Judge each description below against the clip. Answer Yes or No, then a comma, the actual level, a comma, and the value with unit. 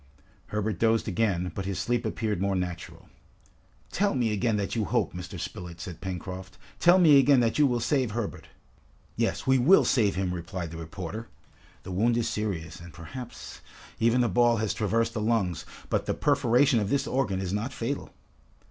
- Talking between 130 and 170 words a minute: No, average, 185 wpm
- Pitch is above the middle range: No, low, 110 Hz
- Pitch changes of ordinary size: Yes, average, 4.7 semitones